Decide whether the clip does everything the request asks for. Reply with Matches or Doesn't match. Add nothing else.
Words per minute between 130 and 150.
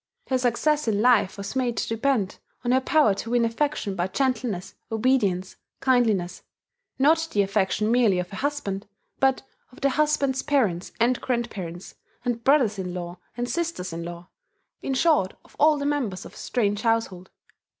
Doesn't match